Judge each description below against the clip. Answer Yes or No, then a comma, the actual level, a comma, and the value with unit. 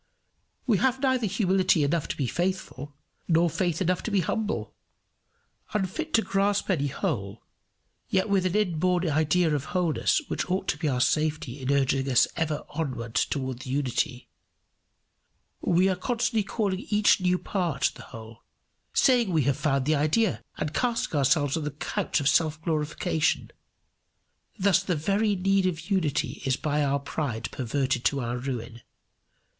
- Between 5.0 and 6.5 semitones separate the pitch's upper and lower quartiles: Yes, wide, 5.4 semitones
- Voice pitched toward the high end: No, medium, 160 Hz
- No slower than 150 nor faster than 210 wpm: Yes, average, 160 wpm